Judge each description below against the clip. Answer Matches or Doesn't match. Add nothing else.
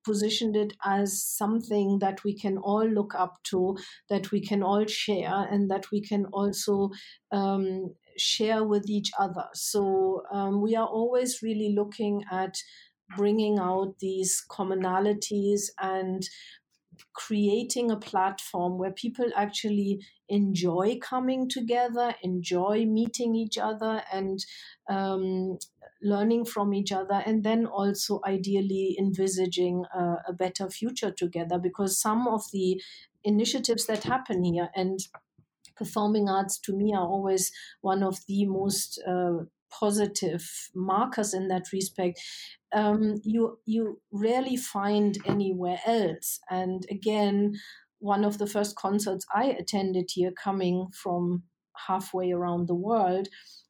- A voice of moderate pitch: Doesn't match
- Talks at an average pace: Doesn't match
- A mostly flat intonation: Matches